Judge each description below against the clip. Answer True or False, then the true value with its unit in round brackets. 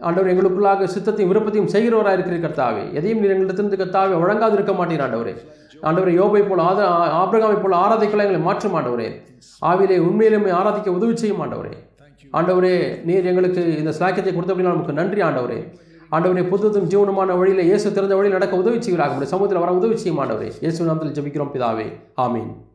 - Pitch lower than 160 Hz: False (185 Hz)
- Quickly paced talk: True (145 wpm)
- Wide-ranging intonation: False (3.4 semitones)